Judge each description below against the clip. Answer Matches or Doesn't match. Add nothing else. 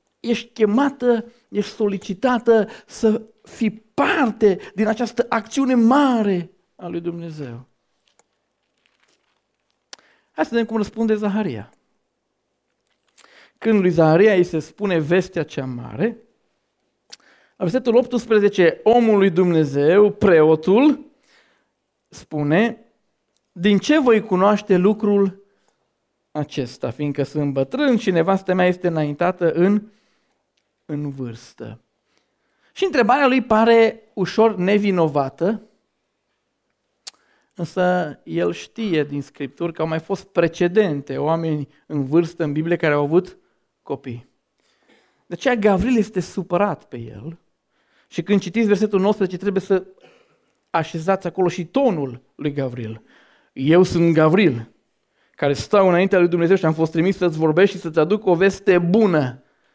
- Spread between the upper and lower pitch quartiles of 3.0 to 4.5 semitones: Doesn't match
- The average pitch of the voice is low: Doesn't match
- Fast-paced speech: Doesn't match